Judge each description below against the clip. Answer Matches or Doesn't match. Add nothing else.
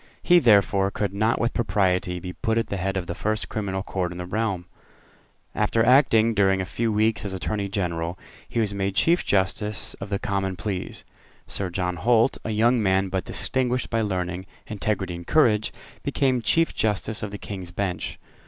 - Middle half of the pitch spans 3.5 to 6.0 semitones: Doesn't match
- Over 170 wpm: Matches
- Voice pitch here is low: Matches